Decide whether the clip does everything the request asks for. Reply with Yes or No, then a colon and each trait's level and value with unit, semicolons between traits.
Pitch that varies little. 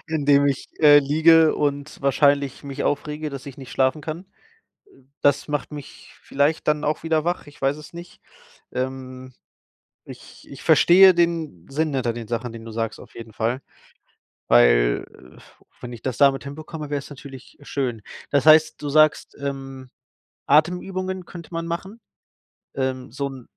No: average, 3.0 semitones